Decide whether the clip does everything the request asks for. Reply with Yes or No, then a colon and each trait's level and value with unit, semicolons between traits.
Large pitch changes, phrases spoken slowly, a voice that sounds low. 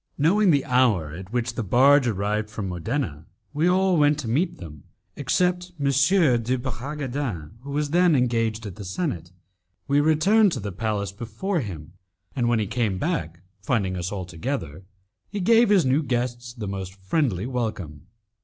No: wide, 6.9 semitones; average, 165 wpm; low, 120 Hz